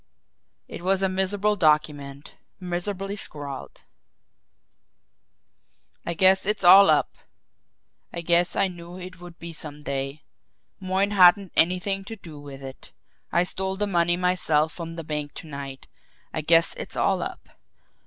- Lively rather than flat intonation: No, average, 3.8 semitones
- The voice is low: No, medium, 175 Hz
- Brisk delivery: No, average, 145 wpm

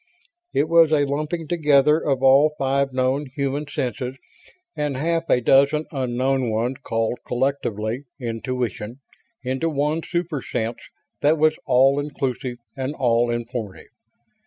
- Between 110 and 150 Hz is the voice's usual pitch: Yes, low, 135 Hz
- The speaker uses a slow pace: Yes, slow, 130 wpm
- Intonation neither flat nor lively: Yes, average, 3.2 semitones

